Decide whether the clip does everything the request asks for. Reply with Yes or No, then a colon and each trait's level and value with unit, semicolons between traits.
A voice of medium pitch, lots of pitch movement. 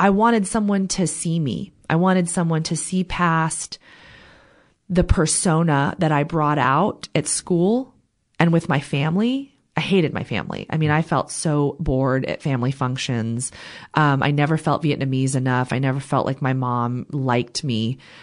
No: medium, 155 Hz; average, 4.8 semitones